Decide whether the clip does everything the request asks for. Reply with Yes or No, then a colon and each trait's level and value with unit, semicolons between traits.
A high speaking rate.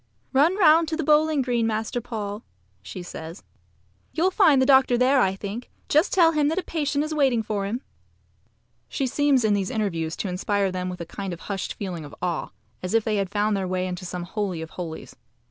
Yes: fast, 215 wpm